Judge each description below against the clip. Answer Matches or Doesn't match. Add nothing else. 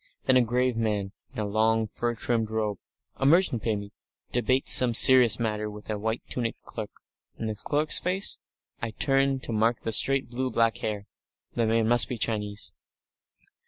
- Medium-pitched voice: Doesn't match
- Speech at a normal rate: Matches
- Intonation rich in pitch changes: Doesn't match